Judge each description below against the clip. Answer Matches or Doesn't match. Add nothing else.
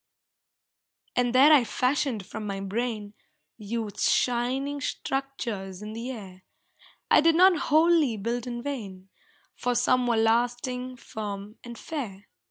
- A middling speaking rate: Doesn't match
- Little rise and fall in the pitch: Doesn't match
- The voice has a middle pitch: Doesn't match